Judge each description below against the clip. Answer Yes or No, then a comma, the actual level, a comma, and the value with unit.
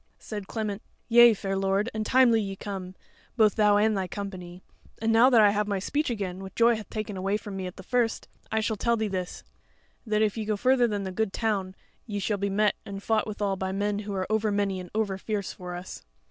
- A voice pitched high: Yes, high, 205 Hz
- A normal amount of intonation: No, narrow, 2.2 semitones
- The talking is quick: Yes, fast, 235 wpm